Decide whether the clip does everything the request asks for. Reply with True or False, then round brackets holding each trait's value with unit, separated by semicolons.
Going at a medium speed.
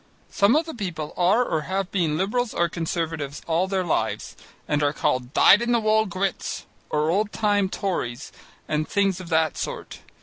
True (180 wpm)